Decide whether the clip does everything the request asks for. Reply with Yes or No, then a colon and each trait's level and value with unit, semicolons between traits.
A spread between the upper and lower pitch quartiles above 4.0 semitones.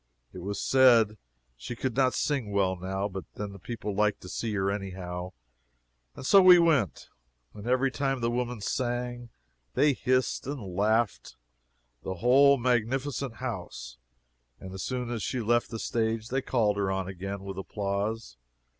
Yes: average, 4.5 semitones